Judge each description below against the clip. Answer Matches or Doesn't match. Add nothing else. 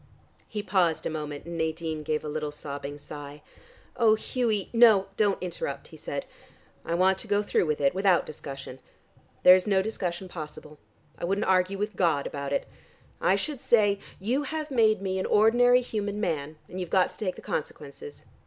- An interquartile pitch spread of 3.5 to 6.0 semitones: Matches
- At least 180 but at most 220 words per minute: Matches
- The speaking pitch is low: Doesn't match